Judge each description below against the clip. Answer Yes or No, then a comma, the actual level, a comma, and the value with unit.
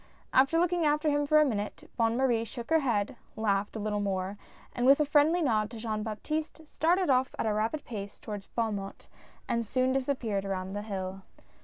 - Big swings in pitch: Yes, wide, 5.8 semitones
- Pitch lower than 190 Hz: No, high, 230 Hz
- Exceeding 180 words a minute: Yes, average, 195 wpm